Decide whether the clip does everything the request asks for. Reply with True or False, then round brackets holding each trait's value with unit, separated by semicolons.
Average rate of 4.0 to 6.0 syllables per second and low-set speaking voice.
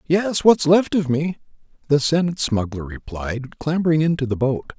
False (5.0 syllables/s; 145 Hz)